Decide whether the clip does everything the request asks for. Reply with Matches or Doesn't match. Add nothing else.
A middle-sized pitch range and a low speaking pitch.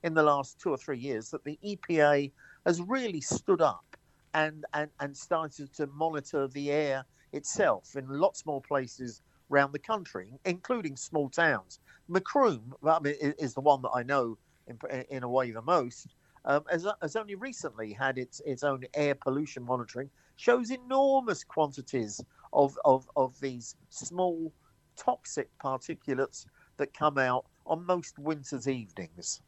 Doesn't match